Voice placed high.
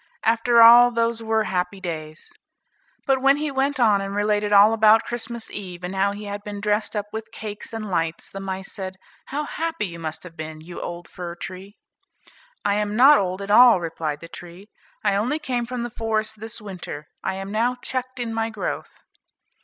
Yes: high, 210 Hz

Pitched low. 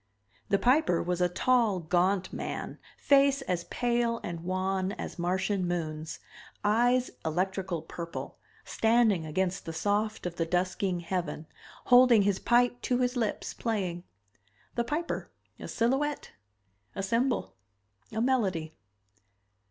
No: high, 195 Hz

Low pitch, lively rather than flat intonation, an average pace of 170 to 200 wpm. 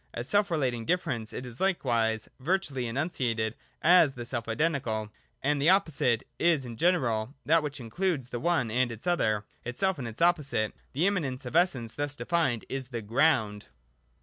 Yes: low, 130 Hz; wide, 6.2 semitones; average, 175 wpm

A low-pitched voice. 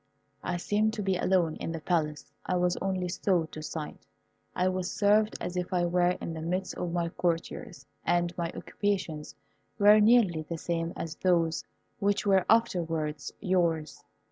No: medium, 175 Hz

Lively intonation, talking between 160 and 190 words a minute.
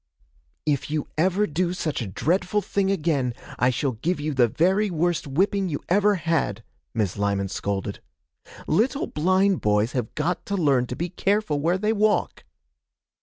Yes: wide, 6.9 semitones; average, 165 wpm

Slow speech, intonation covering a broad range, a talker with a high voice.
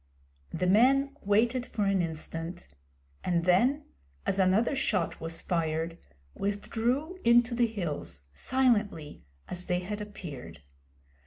Yes: slow, 115 wpm; wide, 6.1 semitones; high, 200 Hz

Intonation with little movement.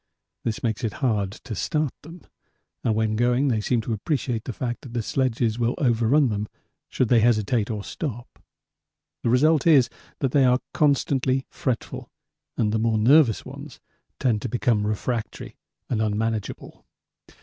No: average, 3.1 semitones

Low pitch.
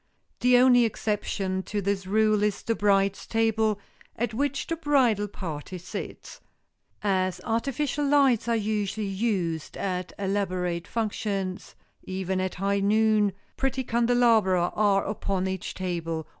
No: high, 205 Hz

